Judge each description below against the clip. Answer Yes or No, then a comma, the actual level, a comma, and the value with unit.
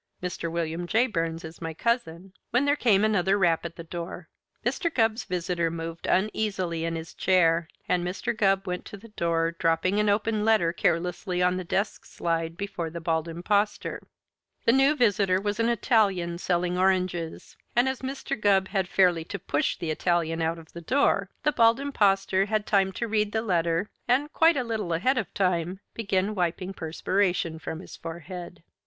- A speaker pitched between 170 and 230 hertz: Yes, medium, 185 Hz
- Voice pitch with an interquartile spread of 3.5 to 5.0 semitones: Yes, average, 4.1 semitones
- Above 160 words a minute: Yes, average, 185 wpm